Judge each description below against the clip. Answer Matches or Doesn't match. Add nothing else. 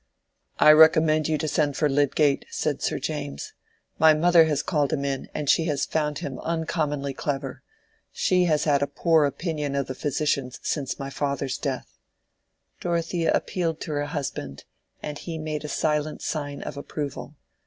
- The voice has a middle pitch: Matches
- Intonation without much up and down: Matches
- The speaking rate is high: Doesn't match